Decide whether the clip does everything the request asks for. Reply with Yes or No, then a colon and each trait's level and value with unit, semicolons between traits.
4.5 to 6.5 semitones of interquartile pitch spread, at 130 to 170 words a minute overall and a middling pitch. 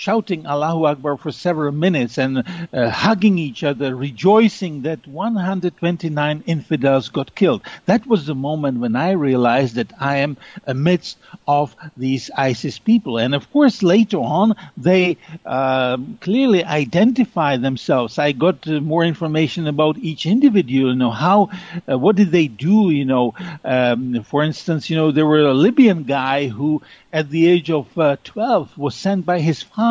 Yes: average, 4.8 semitones; average, 165 wpm; medium, 155 Hz